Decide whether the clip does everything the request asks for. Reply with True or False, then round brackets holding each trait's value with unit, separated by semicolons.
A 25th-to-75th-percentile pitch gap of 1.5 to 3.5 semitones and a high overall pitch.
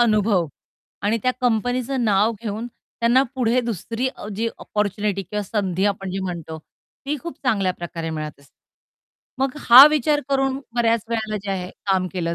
False (4.3 semitones; 215 Hz)